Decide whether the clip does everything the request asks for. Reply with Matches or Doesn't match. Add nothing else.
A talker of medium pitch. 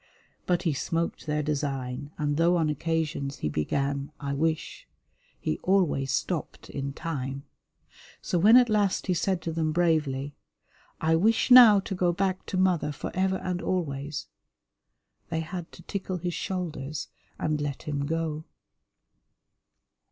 Matches